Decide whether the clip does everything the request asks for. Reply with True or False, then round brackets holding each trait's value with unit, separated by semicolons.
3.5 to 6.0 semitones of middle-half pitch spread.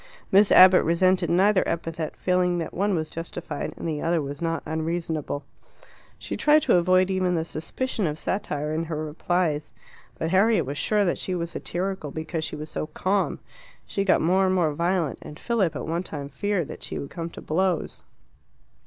False (3.0 semitones)